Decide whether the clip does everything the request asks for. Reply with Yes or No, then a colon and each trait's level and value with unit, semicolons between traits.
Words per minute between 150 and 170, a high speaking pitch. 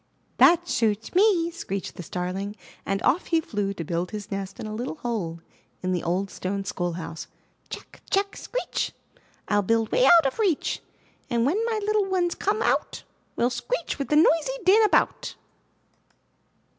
Yes: average, 160 wpm; high, 235 Hz